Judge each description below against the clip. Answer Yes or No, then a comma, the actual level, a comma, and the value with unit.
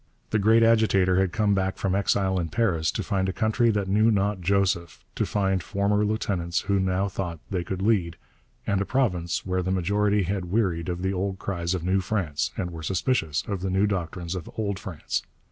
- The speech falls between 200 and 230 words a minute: Yes, fast, 205 wpm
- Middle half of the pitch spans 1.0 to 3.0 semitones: Yes, narrow, 2.5 semitones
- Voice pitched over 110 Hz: No, very low, 95 Hz